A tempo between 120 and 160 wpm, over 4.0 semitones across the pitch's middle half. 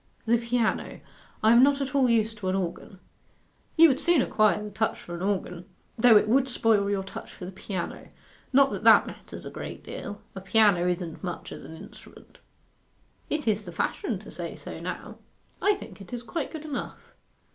No: average, 200 wpm; average, 4.8 semitones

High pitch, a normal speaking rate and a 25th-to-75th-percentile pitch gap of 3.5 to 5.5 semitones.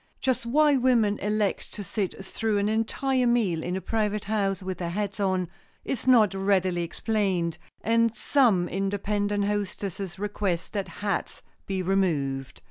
No: high, 205 Hz; average, 145 wpm; average, 2.7 semitones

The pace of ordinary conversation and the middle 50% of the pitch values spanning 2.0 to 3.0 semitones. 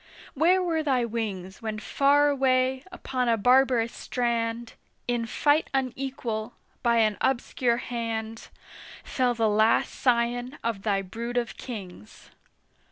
No: slow, 125 wpm; average, 2.7 semitones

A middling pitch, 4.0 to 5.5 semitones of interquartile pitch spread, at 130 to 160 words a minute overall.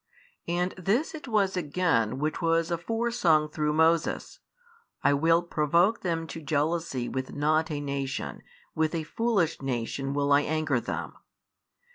No: medium, 160 Hz; average, 3.3 semitones; average, 145 wpm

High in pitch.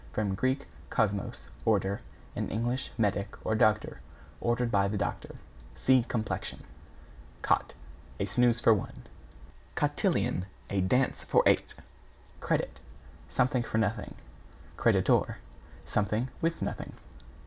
No: low, 110 Hz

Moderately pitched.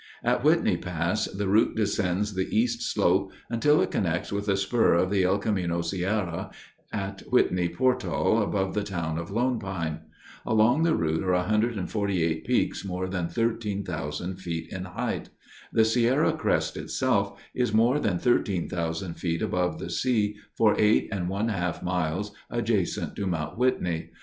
No: very low, 95 Hz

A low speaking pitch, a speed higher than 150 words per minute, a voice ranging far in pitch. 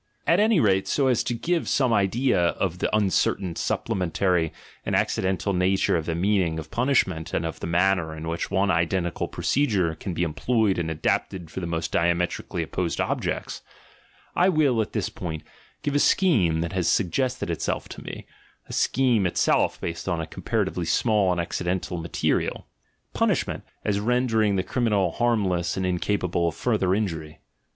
No: very low, 95 Hz; average, 170 wpm; average, 4.7 semitones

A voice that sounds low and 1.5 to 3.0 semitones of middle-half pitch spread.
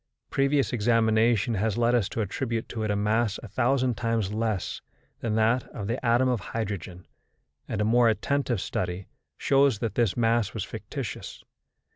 Yes: low, 115 Hz; narrow, 2.4 semitones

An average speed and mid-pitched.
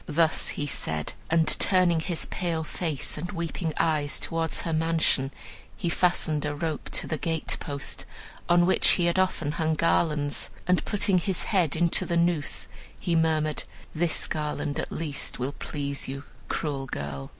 Yes: average, 160 wpm; medium, 160 Hz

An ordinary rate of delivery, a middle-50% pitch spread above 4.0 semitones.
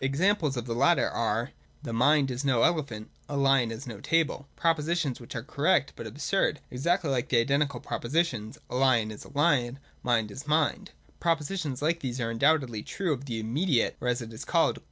No: fast, 215 wpm; average, 4.4 semitones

